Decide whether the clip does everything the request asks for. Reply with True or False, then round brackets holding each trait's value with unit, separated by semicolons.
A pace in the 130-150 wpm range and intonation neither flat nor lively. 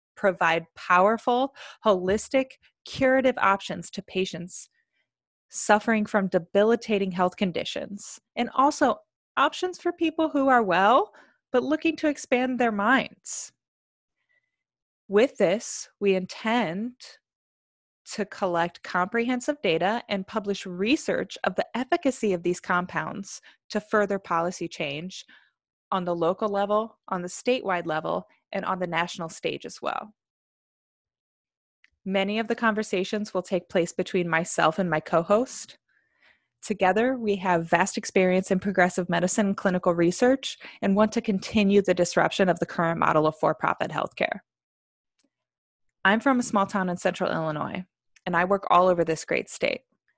True (140 wpm; 4.6 semitones)